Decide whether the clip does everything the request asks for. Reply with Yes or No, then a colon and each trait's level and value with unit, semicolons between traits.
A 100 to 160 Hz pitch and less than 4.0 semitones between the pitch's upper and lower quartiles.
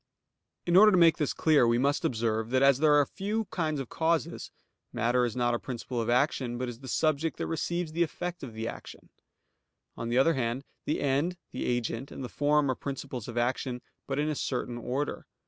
No: low, 135 Hz; average, 4.4 semitones